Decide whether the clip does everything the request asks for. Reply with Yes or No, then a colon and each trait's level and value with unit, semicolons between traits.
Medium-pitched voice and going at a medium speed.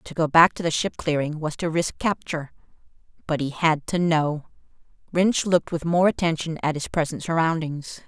Yes: medium, 160 Hz; average, 180 wpm